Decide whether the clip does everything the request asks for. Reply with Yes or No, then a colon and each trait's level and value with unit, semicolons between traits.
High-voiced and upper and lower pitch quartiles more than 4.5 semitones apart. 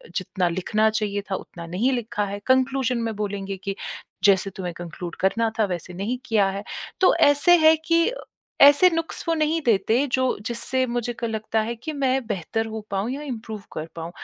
Yes: high, 220 Hz; average, 5.0 semitones